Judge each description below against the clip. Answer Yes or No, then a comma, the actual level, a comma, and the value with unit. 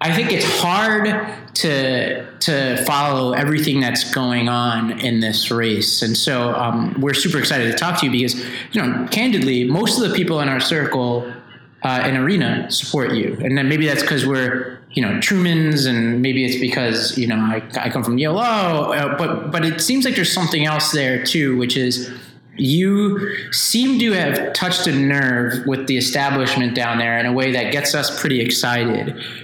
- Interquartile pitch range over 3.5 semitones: Yes, average, 3.9 semitones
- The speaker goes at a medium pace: Yes, average, 190 wpm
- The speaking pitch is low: Yes, low, 130 Hz